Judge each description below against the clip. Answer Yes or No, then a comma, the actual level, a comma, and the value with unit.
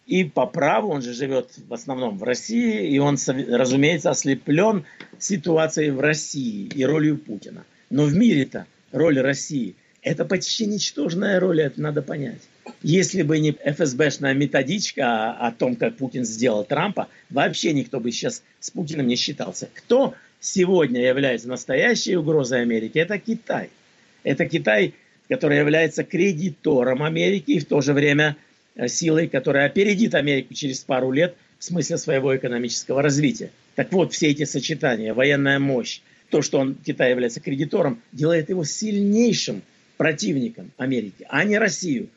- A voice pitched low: No, medium, 150 Hz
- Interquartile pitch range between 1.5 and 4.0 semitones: No, average, 4.6 semitones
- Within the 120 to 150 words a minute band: Yes, average, 145 wpm